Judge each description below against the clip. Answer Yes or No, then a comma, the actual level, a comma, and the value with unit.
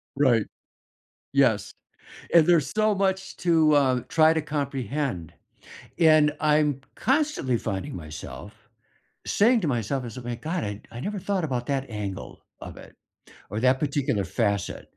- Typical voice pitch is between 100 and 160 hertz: Yes, medium, 140 Hz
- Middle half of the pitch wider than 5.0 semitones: Yes, wide, 5.6 semitones